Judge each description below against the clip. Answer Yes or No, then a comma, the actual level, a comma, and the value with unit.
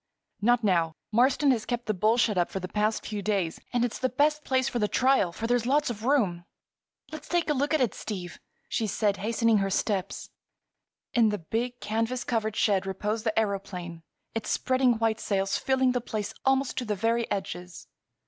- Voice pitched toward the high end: Yes, high, 225 Hz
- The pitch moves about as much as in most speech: Yes, average, 3.8 semitones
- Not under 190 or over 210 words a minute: Yes, average, 195 wpm